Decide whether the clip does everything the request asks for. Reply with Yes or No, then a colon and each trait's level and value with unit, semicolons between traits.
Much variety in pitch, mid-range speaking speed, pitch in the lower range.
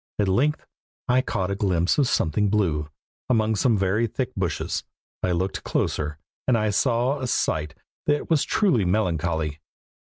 Yes: wide, 6.0 semitones; average, 150 wpm; low, 105 Hz